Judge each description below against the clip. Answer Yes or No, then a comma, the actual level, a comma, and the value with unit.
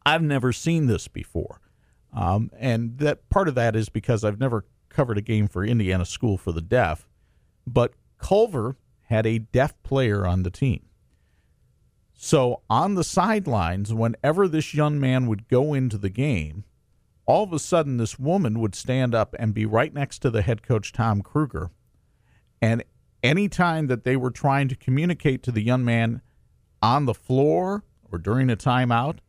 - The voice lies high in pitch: No, low, 125 Hz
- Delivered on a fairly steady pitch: No, average, 4.7 semitones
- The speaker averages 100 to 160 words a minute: No, average, 175 wpm